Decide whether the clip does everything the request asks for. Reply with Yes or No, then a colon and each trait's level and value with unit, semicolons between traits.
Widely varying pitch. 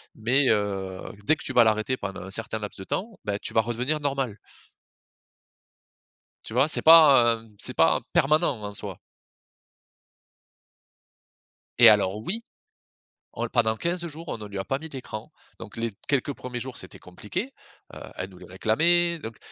Yes: wide, 5.9 semitones